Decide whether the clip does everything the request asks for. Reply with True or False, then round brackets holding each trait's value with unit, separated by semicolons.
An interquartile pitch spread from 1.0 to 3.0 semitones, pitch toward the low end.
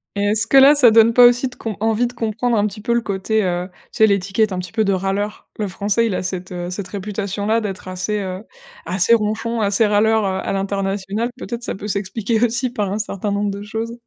False (2.7 semitones; 210 Hz)